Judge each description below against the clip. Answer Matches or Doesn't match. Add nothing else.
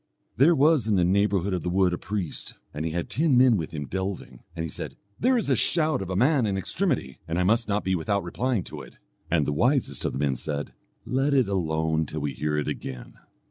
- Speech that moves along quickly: Matches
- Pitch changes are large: Matches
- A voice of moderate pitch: Doesn't match